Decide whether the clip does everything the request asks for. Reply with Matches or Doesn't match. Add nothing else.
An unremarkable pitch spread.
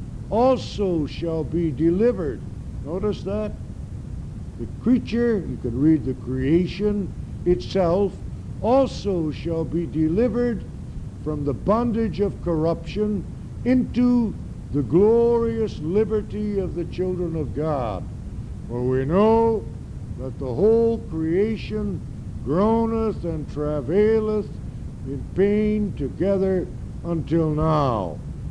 Doesn't match